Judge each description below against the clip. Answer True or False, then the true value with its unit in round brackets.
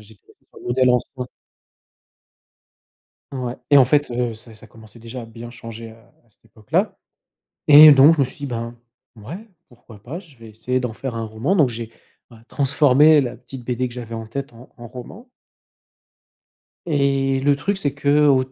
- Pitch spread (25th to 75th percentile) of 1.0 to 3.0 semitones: False (3.5 semitones)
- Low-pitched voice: True (125 Hz)